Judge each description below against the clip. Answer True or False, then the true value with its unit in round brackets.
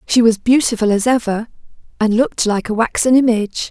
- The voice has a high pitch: True (230 Hz)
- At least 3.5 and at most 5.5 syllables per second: False (5.9 syllables/s)